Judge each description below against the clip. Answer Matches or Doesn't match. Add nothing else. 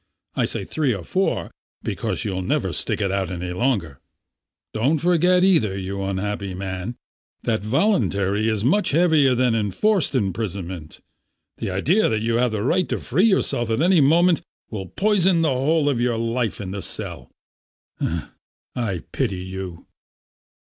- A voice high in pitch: Doesn't match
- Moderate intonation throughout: Doesn't match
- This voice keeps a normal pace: Matches